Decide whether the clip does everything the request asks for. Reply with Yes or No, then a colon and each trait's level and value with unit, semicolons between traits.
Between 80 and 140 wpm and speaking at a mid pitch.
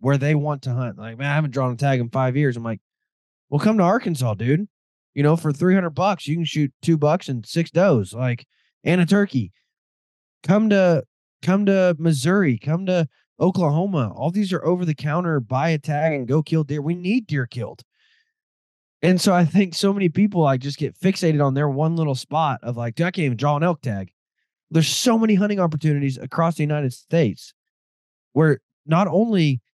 No: fast, 205 wpm; medium, 155 Hz